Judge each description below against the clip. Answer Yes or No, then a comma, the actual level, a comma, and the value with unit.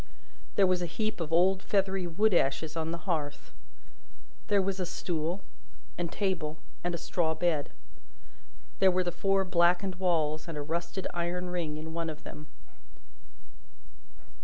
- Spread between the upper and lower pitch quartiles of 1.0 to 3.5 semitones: Yes, average, 2.7 semitones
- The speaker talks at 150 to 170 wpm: Yes, average, 155 wpm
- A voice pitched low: No, medium, 175 Hz